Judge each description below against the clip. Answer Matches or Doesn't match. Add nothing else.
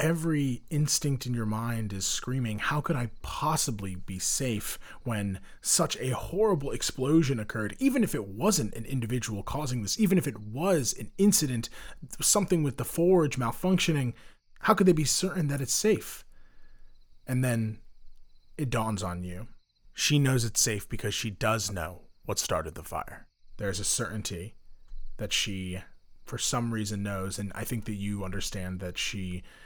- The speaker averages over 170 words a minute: Doesn't match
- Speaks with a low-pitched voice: Matches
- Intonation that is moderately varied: Doesn't match